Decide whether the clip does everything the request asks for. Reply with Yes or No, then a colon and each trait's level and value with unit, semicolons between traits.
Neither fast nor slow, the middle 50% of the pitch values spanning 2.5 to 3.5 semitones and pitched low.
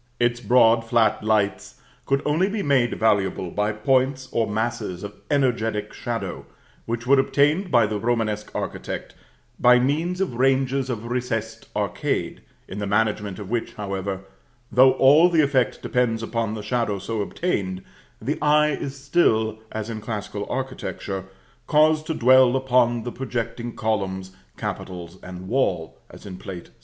No: average, 150 wpm; average, 4.1 semitones; low, 115 Hz